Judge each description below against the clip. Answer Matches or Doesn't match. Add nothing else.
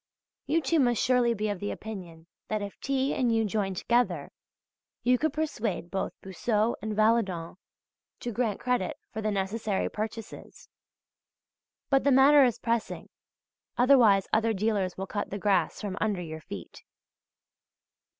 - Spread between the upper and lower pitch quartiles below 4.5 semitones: Matches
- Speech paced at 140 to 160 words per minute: Matches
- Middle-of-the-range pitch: Doesn't match